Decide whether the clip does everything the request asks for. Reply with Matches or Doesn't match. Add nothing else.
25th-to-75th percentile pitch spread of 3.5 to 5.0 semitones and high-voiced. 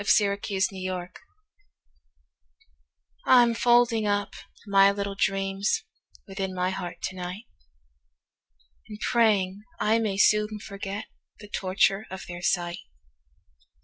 Doesn't match